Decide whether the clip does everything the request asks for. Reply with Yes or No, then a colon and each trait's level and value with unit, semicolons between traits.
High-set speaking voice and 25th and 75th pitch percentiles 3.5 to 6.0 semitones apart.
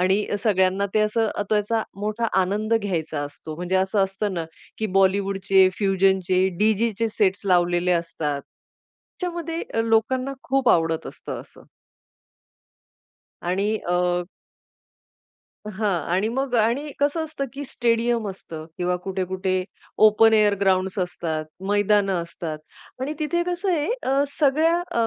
Yes: high, 205 Hz; average, 4.0 semitones